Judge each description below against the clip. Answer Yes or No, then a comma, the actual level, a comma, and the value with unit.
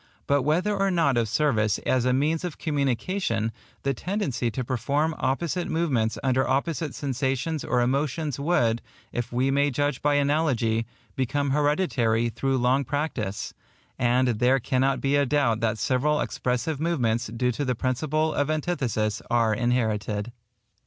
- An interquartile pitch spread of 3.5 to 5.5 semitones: Yes, average, 3.8 semitones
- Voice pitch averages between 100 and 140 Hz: Yes, low, 135 Hz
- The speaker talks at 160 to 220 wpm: No, average, 150 wpm